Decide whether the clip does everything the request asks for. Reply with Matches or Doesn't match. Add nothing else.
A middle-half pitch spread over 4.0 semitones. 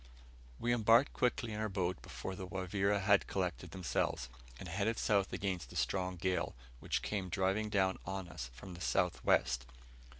Doesn't match